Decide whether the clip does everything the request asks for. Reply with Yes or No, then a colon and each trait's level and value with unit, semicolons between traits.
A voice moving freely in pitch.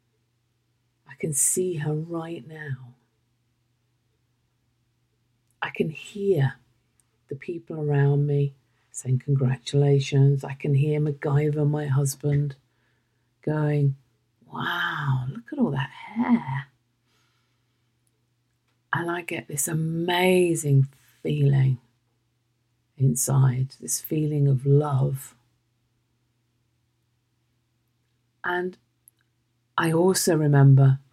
No: average, 3.5 semitones